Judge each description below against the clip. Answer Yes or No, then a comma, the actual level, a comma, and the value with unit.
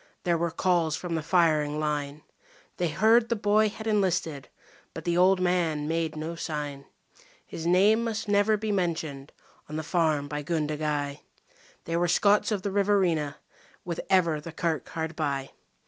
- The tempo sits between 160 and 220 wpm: Yes, average, 165 wpm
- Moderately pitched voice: Yes, medium, 165 Hz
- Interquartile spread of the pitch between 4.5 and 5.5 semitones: No, average, 4.0 semitones